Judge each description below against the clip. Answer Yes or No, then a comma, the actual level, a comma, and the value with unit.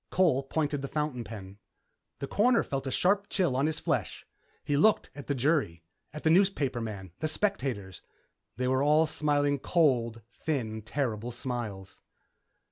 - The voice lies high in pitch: No, medium, 140 Hz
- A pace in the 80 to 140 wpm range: No, average, 150 wpm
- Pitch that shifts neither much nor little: Yes, average, 5.0 semitones